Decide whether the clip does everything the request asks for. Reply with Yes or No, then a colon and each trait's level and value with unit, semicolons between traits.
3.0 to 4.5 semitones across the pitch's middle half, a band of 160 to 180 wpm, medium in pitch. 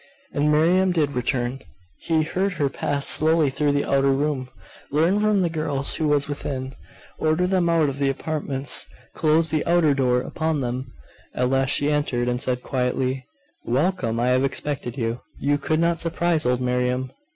Yes: average, 3.6 semitones; average, 175 wpm; medium, 145 Hz